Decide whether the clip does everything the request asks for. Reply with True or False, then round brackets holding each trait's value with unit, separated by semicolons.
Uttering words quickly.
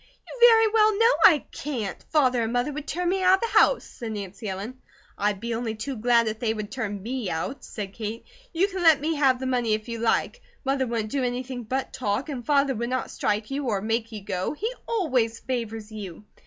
True (225 wpm)